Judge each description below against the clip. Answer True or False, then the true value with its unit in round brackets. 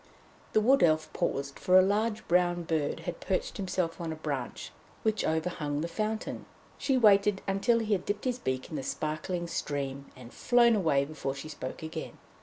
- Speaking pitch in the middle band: True (175 Hz)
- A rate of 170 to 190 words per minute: True (185 wpm)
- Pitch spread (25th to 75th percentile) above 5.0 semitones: True (5.5 semitones)